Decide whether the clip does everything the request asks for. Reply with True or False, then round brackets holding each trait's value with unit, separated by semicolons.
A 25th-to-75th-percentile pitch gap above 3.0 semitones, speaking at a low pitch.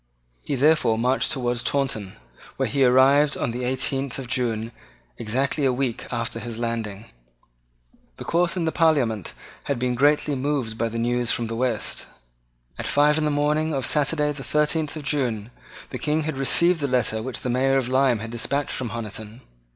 True (3.9 semitones; 130 Hz)